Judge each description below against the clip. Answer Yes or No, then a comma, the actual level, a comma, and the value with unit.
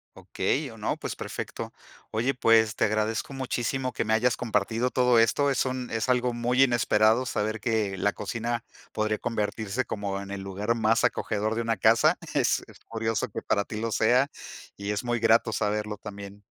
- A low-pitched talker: Yes, low, 115 Hz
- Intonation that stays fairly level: Yes, narrow, 2.2 semitones